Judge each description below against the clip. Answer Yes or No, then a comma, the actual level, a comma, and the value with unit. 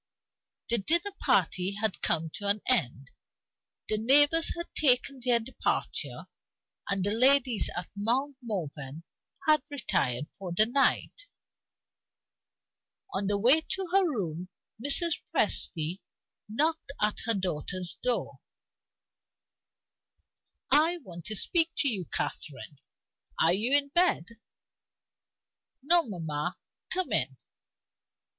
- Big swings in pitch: Yes, wide, 8.0 semitones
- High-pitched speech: Yes, high, 220 Hz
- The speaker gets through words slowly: Yes, slow, 110 wpm